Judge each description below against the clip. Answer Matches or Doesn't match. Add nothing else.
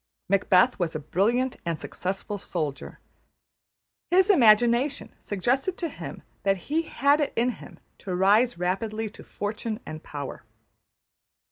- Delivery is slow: Matches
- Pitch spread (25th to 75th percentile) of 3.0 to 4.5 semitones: Doesn't match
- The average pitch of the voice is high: Matches